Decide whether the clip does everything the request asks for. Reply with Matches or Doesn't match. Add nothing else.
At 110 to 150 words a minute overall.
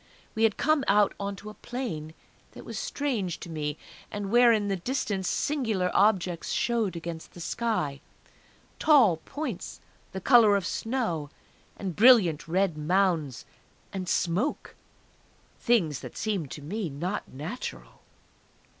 Matches